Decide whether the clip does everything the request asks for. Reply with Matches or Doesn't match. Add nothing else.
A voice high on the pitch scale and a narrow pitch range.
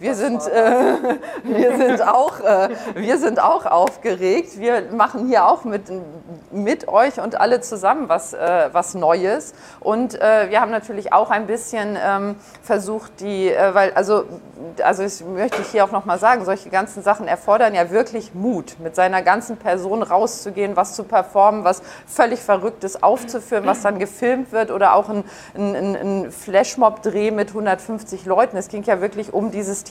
Matches